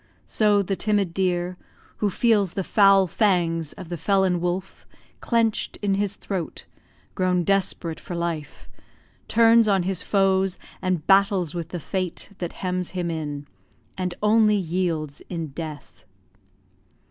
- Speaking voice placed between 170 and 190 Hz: Yes, medium, 185 Hz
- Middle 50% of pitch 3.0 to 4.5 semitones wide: No, narrow, 2.6 semitones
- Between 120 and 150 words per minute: Yes, slow, 135 wpm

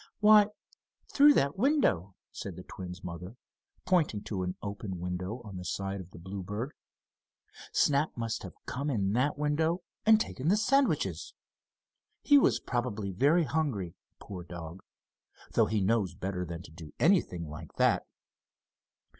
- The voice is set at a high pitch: No, low, 105 Hz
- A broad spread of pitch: Yes, wide, 8.7 semitones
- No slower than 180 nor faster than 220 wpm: No, average, 145 wpm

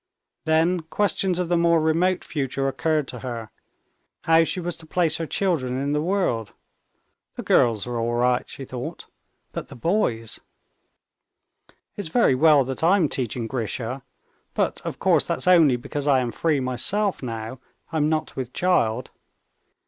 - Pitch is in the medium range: Yes, medium, 145 Hz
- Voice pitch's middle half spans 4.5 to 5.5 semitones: Yes, average, 5.2 semitones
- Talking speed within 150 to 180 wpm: Yes, average, 155 wpm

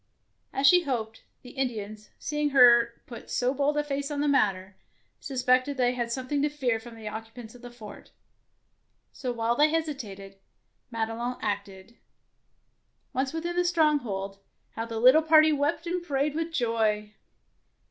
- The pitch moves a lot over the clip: No, average, 4.6 semitones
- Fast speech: No, average, 160 wpm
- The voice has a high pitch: Yes, very high, 250 Hz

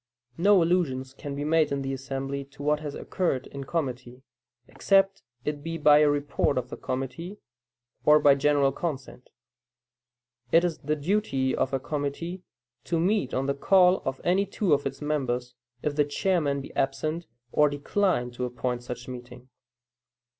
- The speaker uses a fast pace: No, average, 165 wpm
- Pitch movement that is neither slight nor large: Yes, average, 3.8 semitones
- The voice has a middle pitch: Yes, medium, 145 Hz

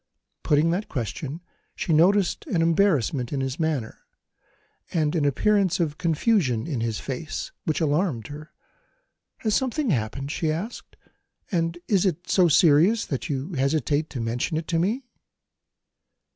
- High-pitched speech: No, medium, 160 Hz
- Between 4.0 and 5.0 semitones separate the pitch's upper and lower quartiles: Yes, average, 4.5 semitones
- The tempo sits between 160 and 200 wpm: No, average, 145 wpm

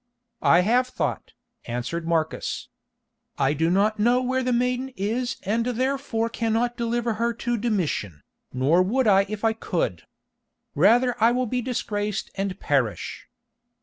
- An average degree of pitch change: Yes, average, 4.8 semitones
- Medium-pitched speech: No, high, 225 Hz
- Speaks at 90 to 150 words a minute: Yes, average, 145 wpm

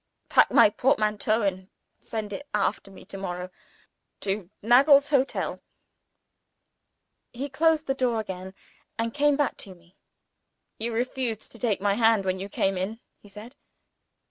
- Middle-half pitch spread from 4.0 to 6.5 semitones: Yes, average, 4.6 semitones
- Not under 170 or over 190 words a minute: No, average, 150 wpm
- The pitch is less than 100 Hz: No, high, 220 Hz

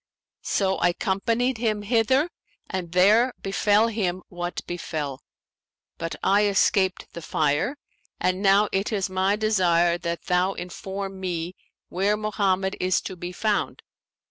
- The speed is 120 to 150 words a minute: Yes, slow, 135 wpm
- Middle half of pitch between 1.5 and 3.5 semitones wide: Yes, average, 3.0 semitones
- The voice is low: No, high, 190 Hz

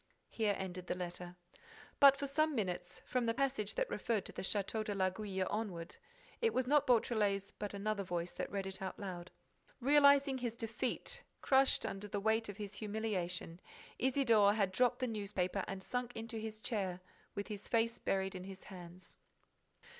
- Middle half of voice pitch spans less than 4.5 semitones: Yes, average, 4.0 semitones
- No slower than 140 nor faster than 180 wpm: Yes, average, 170 wpm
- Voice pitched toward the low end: No, high, 210 Hz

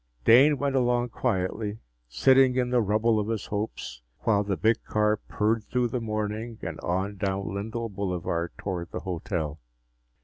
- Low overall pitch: Yes, low, 105 Hz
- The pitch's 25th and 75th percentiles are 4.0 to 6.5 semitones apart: No, average, 3.5 semitones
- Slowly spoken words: No, average, 160 wpm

